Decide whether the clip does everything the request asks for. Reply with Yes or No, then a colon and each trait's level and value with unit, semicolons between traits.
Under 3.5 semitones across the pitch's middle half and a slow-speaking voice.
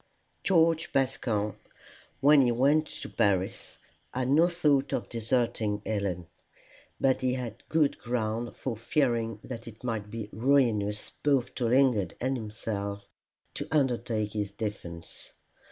No: average, 4.1 semitones; slow, 130 wpm